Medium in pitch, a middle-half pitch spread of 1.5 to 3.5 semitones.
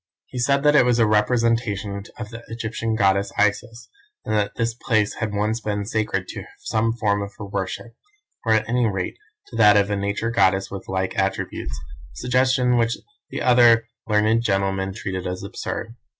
No: low, 110 Hz; average, 2.7 semitones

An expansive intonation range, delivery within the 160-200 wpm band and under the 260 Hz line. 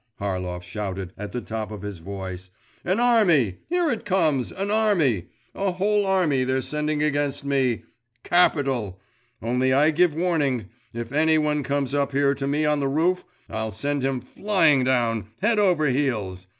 Yes: wide, 6.6 semitones; average, 165 wpm; medium, 140 Hz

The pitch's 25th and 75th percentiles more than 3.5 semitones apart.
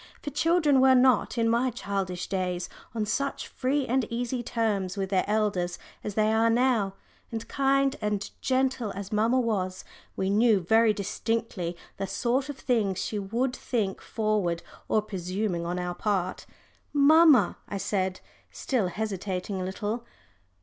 Yes: average, 4.4 semitones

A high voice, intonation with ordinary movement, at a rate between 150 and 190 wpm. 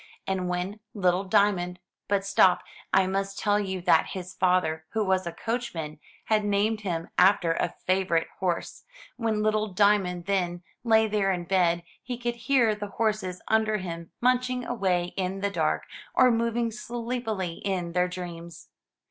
Yes: high, 195 Hz; average, 3.3 semitones; average, 165 wpm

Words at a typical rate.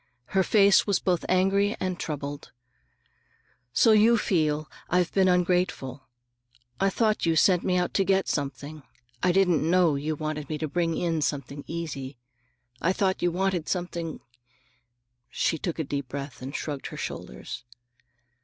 Yes: average, 155 wpm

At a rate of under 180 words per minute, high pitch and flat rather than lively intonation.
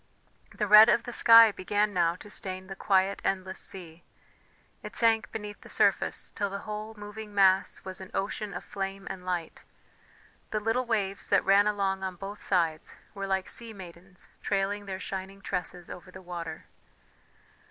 Yes: average, 170 wpm; high, 195 Hz; narrow, 2.0 semitones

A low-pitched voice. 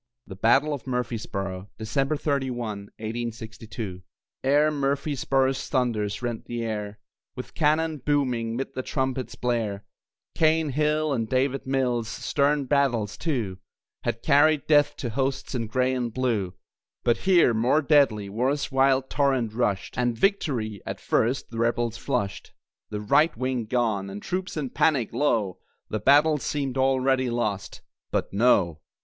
Yes: low, 125 Hz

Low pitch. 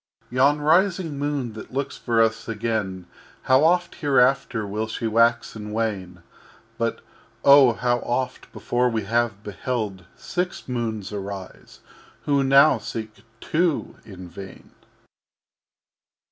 Yes: low, 115 Hz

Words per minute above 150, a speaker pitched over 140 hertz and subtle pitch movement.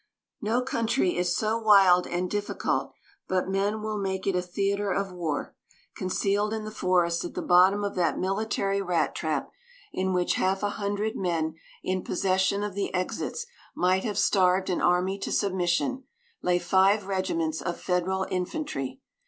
Yes: average, 160 wpm; high, 190 Hz; narrow, 2.2 semitones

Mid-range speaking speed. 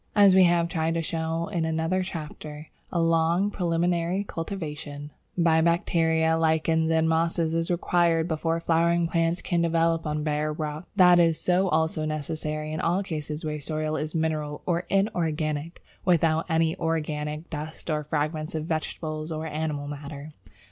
Yes: average, 155 wpm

